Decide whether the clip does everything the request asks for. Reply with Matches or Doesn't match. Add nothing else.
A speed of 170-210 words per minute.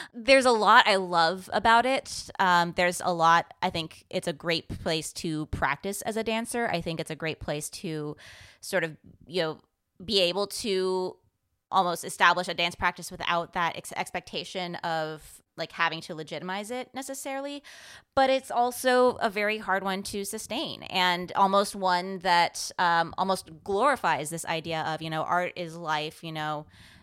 Matches